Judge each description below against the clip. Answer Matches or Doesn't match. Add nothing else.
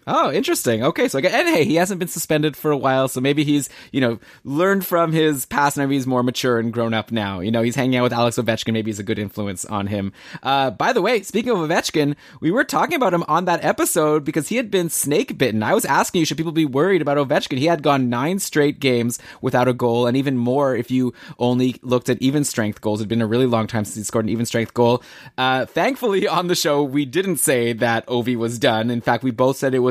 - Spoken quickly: Matches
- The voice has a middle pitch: Doesn't match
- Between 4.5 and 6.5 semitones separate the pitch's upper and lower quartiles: Matches